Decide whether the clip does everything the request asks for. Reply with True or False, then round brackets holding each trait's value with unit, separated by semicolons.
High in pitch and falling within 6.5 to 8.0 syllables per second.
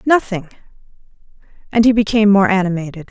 True (205 Hz; 6.7 syllables/s)